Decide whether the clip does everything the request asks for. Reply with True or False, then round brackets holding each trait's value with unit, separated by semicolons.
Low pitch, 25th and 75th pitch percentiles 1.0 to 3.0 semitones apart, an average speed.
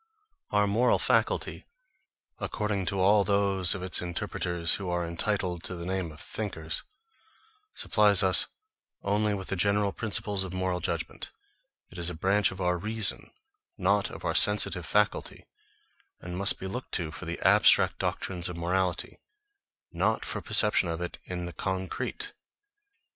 True (95 Hz; 2.5 semitones; 155 wpm)